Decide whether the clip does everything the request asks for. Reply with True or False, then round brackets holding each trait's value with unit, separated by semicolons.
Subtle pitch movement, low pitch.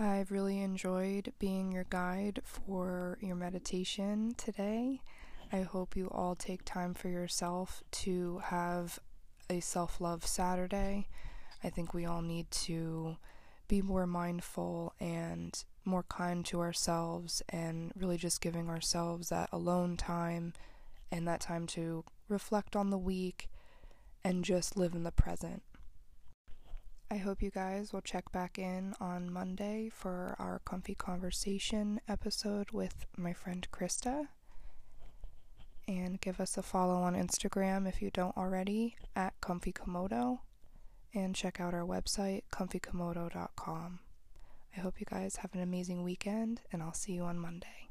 False (2.0 semitones; 185 Hz)